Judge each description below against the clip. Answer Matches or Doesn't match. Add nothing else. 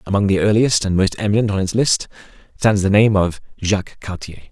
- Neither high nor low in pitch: Doesn't match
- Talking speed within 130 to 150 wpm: Doesn't match